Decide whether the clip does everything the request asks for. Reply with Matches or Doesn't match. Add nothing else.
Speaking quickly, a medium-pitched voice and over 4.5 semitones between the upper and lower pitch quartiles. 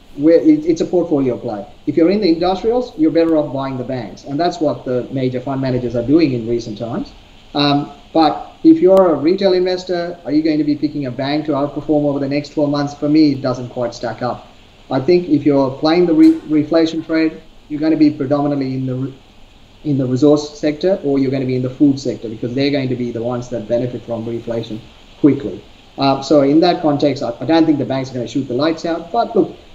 Doesn't match